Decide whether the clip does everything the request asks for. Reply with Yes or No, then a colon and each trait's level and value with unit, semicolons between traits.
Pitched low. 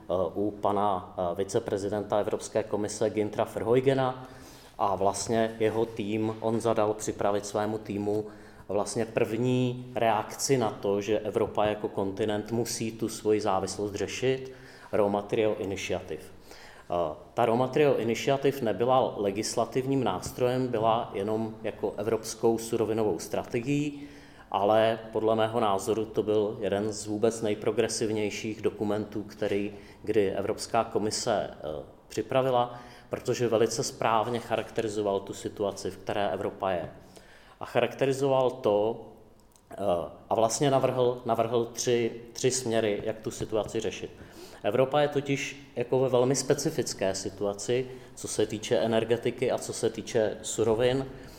Yes: low, 110 Hz